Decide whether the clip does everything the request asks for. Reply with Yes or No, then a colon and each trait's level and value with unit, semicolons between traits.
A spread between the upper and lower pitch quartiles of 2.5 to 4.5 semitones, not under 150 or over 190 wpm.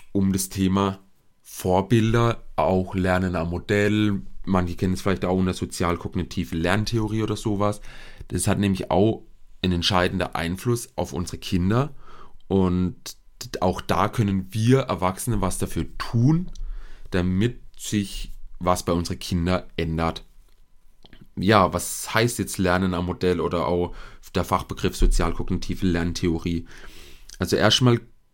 No: average, 2.9 semitones; slow, 125 wpm